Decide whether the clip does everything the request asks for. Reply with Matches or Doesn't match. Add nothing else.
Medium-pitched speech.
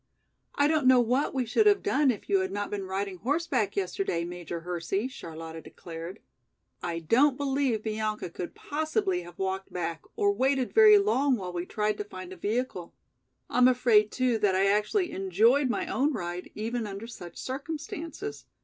Doesn't match